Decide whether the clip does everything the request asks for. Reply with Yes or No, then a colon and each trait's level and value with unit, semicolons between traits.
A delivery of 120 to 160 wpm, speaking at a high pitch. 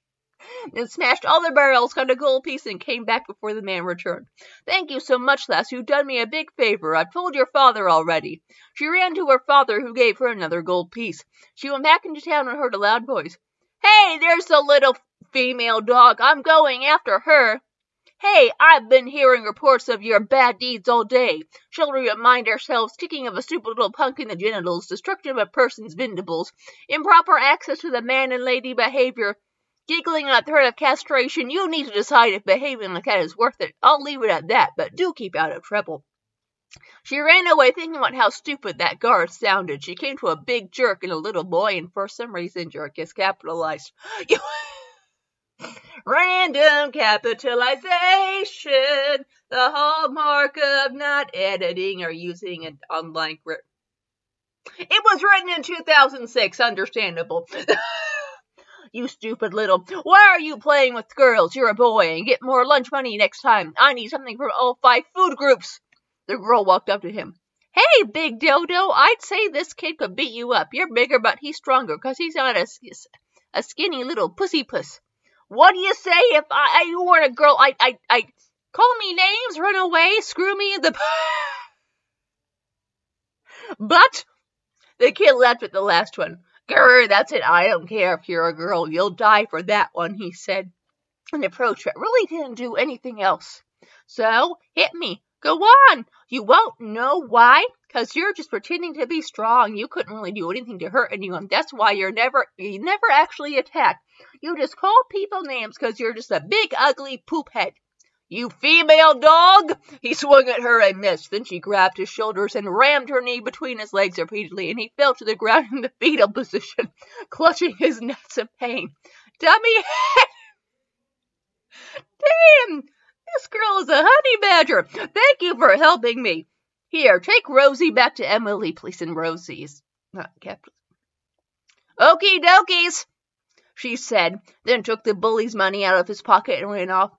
No: average, 180 wpm; very high, 270 Hz